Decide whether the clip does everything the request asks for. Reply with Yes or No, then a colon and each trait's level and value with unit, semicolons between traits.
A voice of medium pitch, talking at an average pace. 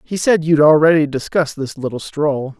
Yes: medium, 150 Hz; average, 185 wpm